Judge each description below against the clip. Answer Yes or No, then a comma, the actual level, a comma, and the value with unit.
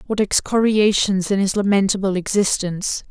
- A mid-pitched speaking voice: No, high, 200 Hz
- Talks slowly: Yes, slow, 115 wpm